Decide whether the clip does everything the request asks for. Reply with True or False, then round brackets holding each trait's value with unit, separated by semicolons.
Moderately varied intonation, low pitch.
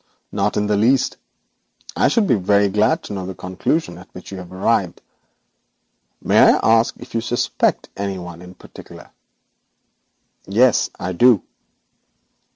True (3.7 semitones; 100 Hz)